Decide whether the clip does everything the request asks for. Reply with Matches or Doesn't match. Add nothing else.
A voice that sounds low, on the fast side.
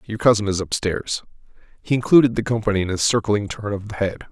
Matches